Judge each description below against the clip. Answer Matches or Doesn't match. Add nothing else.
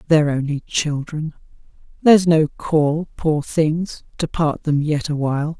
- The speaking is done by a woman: Matches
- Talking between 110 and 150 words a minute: Matches